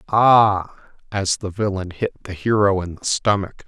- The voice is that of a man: Yes, male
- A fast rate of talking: No, average, 165 wpm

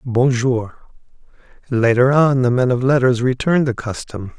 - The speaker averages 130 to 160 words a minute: Yes, slow, 135 wpm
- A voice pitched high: No, low, 125 Hz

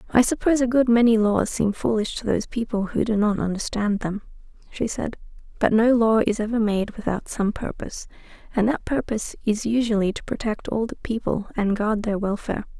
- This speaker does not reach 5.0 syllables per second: No, 5.6 syllables/s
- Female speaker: Yes, female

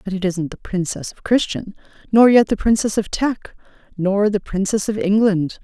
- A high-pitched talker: Yes, high, 200 Hz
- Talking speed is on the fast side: No, average, 190 wpm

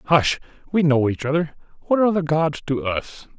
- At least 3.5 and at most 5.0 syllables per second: No, 5.3 syllables/s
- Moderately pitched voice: Yes, medium, 155 Hz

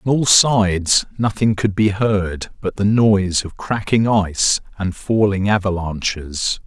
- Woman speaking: No, male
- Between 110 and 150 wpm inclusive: Yes, average, 145 wpm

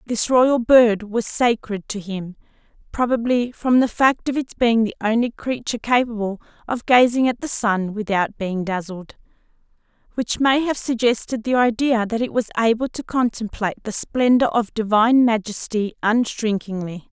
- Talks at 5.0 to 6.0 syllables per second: No, 4.8 syllables/s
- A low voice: No, high, 225 Hz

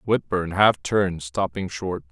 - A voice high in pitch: No, very low, 95 Hz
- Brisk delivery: No, average, 140 wpm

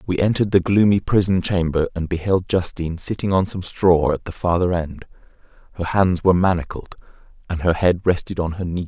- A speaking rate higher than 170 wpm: Yes, average, 190 wpm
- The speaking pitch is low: Yes, very low, 90 Hz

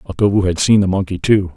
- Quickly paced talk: Yes, fast, 230 wpm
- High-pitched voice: No, very low, 95 Hz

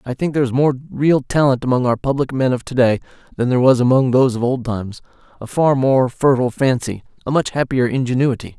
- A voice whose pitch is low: Yes, low, 130 Hz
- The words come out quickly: Yes, fast, 210 wpm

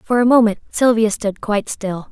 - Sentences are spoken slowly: No, average, 200 wpm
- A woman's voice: Yes, female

